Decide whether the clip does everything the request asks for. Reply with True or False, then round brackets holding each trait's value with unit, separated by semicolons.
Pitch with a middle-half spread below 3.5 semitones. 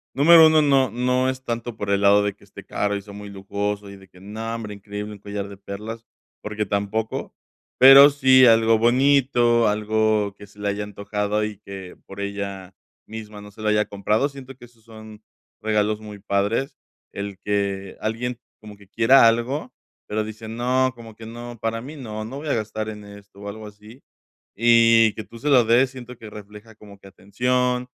True (2.8 semitones)